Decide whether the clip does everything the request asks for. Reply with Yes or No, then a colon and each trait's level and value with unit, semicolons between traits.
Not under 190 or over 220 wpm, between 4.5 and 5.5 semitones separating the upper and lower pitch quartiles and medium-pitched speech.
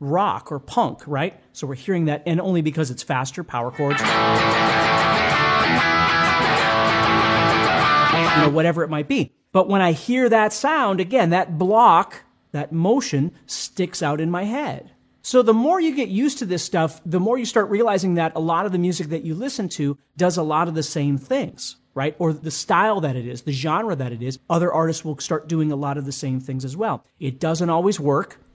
Yes: fast, 205 wpm; average, 5.0 semitones; medium, 160 Hz